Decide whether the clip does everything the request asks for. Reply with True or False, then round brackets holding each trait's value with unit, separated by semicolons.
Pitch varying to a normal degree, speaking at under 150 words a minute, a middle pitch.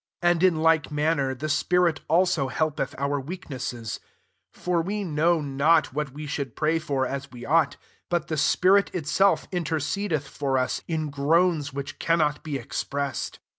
False (3.1 semitones; 165 wpm; 155 Hz)